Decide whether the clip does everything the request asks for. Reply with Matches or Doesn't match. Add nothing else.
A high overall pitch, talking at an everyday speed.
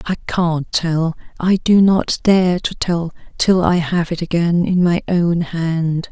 Doesn't match